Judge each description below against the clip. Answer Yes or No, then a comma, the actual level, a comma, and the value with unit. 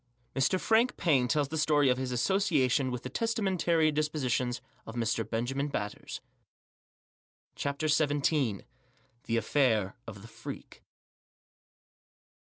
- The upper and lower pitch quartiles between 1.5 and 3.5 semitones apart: No, average, 4.2 semitones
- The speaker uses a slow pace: Yes, slow, 120 wpm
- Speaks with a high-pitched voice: No, medium, 140 Hz